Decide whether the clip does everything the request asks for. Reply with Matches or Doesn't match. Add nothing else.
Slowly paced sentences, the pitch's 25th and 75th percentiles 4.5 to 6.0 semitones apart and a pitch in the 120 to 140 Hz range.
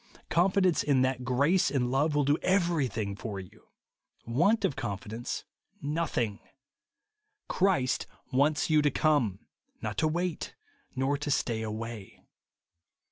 Matches